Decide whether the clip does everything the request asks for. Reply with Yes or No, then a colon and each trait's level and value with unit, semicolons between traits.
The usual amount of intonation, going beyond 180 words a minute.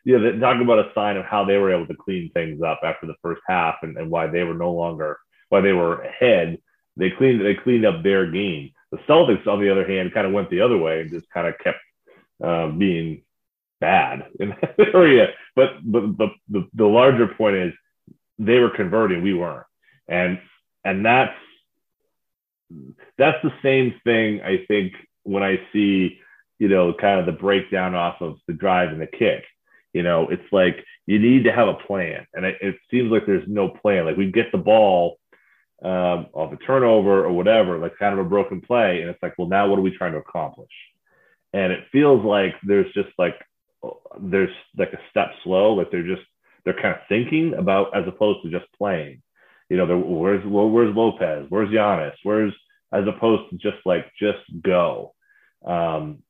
Yes: average, 3.6 semitones; average, 200 wpm